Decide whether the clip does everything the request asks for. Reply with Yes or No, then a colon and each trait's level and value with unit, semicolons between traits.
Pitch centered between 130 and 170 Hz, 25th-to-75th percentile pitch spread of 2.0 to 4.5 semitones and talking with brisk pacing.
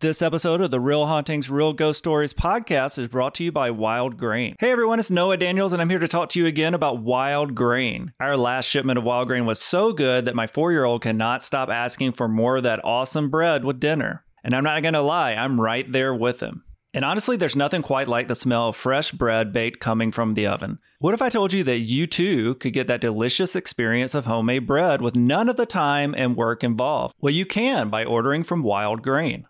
No: low, 135 Hz; average, 5.0 semitones; fast, 235 wpm